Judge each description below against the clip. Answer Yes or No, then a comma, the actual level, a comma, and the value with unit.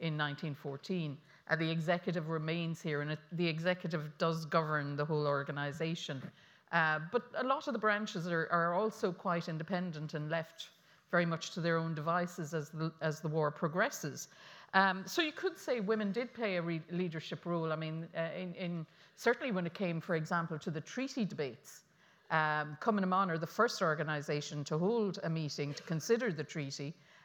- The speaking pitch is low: No, medium, 165 Hz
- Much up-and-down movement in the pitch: No, average, 2.9 semitones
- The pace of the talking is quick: No, average, 185 wpm